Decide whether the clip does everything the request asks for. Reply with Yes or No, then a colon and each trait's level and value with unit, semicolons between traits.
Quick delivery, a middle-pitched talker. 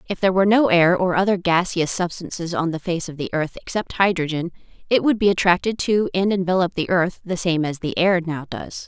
Yes: fast, 225 wpm; medium, 180 Hz